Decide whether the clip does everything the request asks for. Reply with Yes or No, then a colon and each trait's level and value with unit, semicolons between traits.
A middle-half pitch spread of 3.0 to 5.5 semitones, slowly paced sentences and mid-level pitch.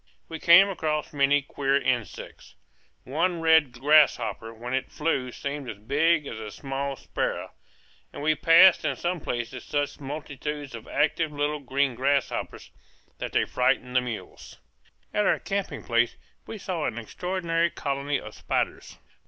No: average, 3.9 semitones; average, 150 wpm; medium, 145 Hz